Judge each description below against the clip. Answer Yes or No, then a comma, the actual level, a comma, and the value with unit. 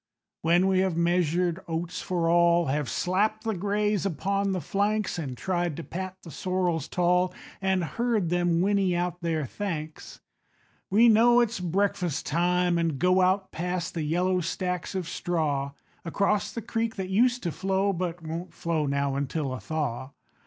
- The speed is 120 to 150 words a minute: No, average, 165 wpm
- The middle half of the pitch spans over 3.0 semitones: No, average, 2.7 semitones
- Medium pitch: Yes, medium, 180 Hz